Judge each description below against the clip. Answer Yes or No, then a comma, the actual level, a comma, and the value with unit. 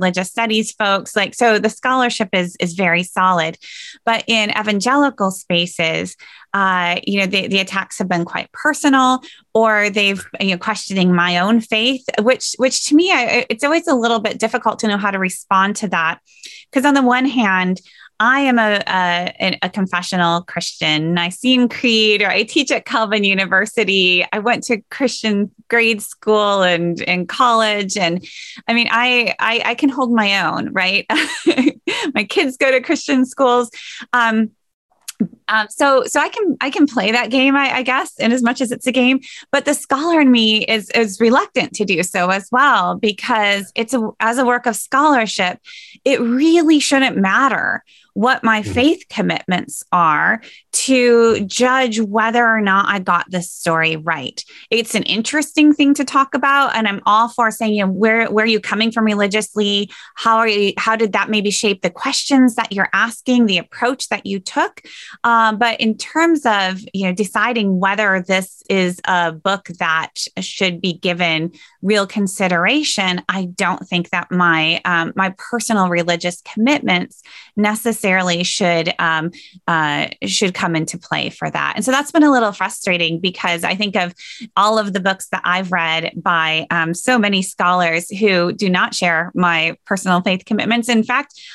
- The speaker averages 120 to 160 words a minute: No, average, 175 wpm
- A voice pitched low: No, high, 215 Hz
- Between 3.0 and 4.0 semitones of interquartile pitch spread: No, average, 4.8 semitones